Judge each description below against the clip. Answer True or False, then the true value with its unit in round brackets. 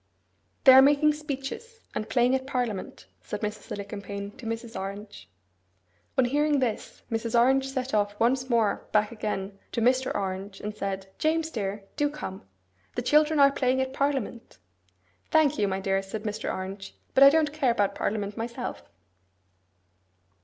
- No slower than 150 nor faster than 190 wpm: True (160 wpm)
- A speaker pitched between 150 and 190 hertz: False (235 Hz)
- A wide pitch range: False (4.8 semitones)